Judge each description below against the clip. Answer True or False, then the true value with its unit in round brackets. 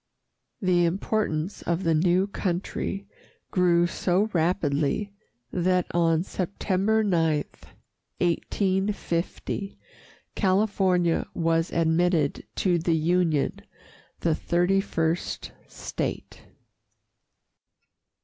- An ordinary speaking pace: False (80 wpm)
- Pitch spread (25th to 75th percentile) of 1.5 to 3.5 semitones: True (2.6 semitones)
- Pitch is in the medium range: True (175 Hz)